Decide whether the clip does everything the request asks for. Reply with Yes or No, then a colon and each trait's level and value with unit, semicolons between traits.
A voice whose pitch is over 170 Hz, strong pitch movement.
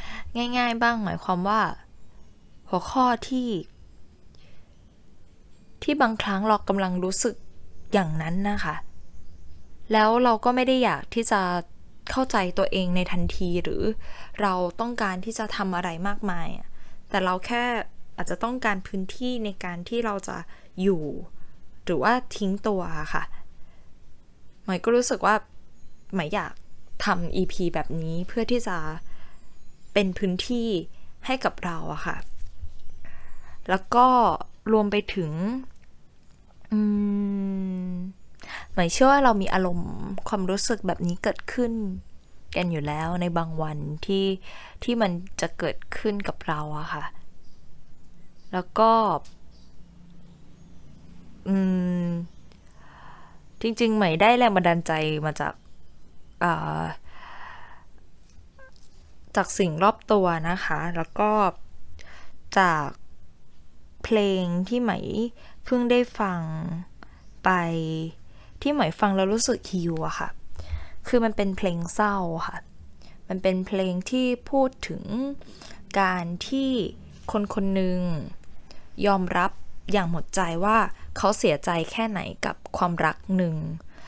Yes: medium, 185 Hz; wide, 6.4 semitones